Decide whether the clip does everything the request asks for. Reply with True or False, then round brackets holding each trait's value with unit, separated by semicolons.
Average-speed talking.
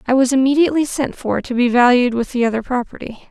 False (220 wpm)